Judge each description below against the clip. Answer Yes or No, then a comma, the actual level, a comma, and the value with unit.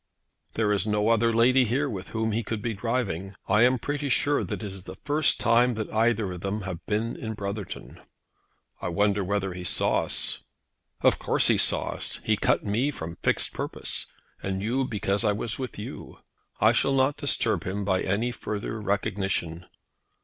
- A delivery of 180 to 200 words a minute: Yes, average, 185 wpm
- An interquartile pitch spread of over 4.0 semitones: No, average, 3.3 semitones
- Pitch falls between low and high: No, low, 105 Hz